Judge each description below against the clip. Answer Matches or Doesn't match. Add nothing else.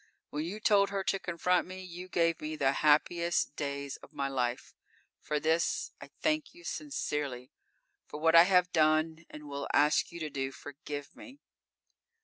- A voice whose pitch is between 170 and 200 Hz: Doesn't match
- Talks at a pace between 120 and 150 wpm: Doesn't match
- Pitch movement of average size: Matches